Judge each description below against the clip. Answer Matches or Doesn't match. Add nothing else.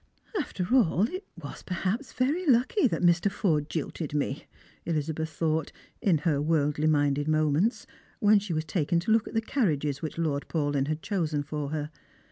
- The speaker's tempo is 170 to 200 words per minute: Matches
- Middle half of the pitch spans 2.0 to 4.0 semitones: Doesn't match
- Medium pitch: Matches